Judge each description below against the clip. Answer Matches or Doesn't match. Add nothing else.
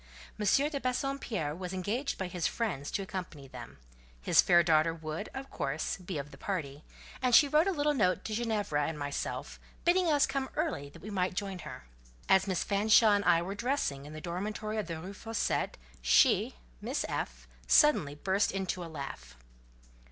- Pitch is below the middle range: Doesn't match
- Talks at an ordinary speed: Matches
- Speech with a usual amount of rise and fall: Doesn't match